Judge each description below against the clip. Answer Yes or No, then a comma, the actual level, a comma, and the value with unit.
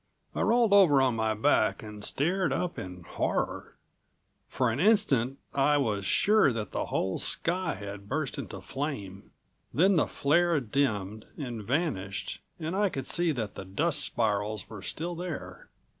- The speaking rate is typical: Yes, average, 160 wpm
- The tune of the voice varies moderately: No, wide, 8.2 semitones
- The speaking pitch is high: No, low, 135 Hz